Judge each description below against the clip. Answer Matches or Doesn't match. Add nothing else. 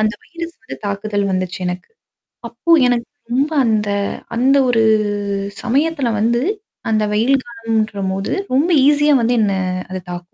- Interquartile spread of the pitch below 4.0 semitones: Doesn't match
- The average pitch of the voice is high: Matches